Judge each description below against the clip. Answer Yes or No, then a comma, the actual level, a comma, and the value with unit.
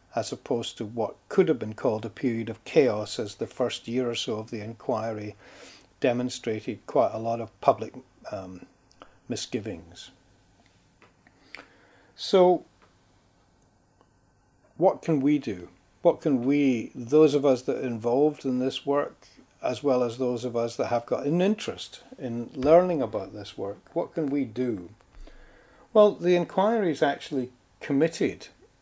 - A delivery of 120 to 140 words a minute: No, average, 150 wpm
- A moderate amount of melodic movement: Yes, average, 4.8 semitones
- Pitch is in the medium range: No, low, 120 Hz